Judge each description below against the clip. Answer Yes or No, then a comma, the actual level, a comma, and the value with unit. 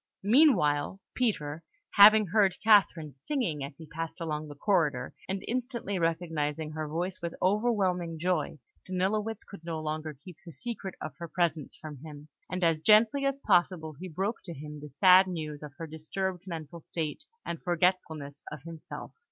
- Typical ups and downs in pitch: Yes, average, 4.0 semitones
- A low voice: No, medium, 170 Hz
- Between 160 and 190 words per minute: Yes, average, 165 wpm